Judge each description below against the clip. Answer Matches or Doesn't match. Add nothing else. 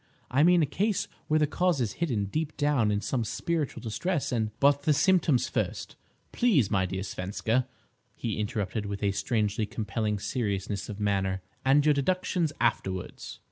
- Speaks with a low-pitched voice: Matches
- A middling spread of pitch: Doesn't match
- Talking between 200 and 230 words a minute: Doesn't match